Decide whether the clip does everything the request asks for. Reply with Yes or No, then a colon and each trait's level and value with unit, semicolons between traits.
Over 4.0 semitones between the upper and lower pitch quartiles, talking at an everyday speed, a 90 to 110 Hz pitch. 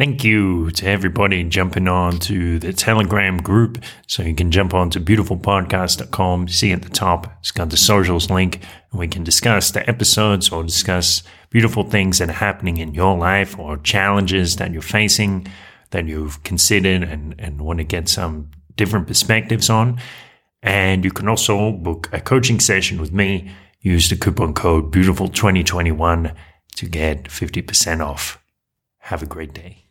No: average, 3.0 semitones; average, 165 wpm; very low, 95 Hz